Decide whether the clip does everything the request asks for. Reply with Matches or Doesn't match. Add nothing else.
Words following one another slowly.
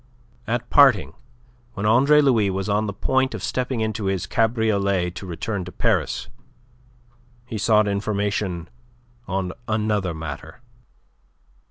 Matches